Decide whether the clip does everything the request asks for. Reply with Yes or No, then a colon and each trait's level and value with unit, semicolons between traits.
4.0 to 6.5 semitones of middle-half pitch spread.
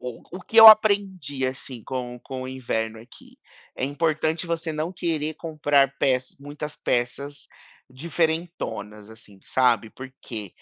Yes: average, 4.5 semitones